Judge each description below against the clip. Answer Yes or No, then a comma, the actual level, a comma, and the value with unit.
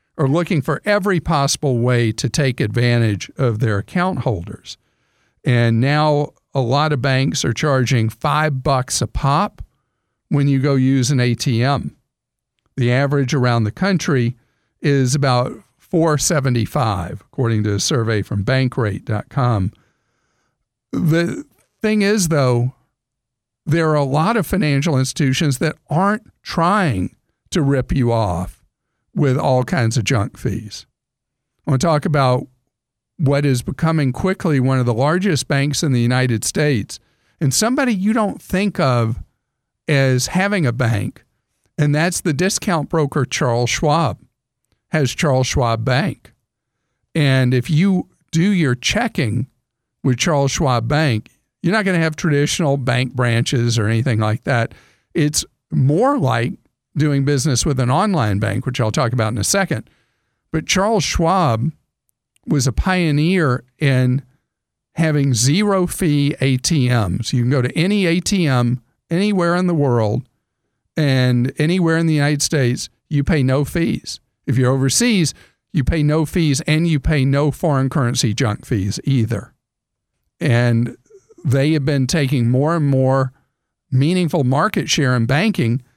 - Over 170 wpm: No, average, 145 wpm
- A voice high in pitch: No, low, 135 Hz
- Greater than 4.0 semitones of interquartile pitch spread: Yes, average, 4.5 semitones